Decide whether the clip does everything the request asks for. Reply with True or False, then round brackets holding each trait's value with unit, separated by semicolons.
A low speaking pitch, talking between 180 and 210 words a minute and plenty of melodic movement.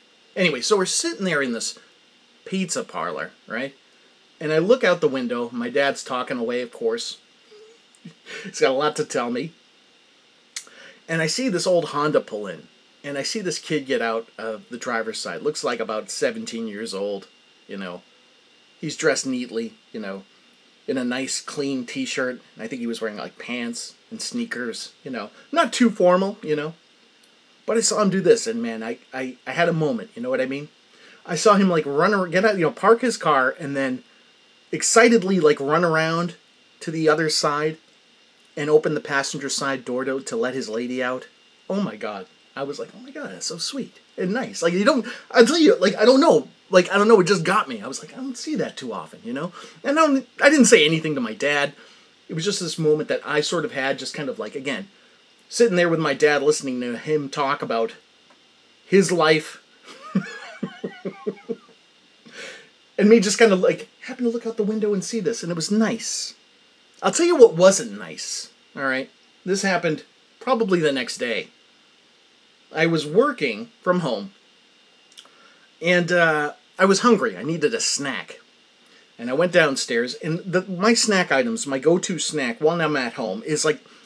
False (185 Hz; 200 wpm; 7.6 semitones)